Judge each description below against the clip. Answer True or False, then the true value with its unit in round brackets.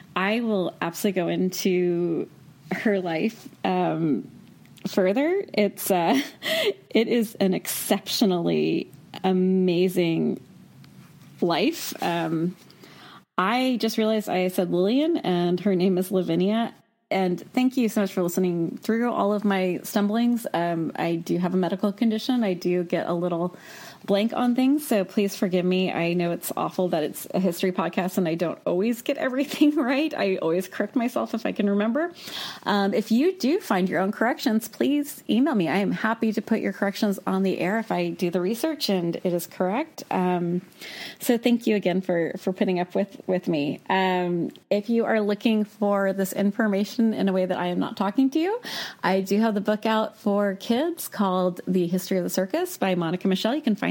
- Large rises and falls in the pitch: False (3.9 semitones)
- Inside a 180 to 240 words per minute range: True (185 wpm)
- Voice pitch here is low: False (195 Hz)